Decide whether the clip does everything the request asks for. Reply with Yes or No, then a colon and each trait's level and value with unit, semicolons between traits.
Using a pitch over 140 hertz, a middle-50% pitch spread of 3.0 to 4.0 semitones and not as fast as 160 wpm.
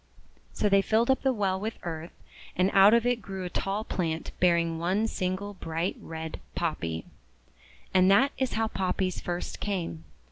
No: high, 190 Hz; average, 3.6 semitones; average, 170 wpm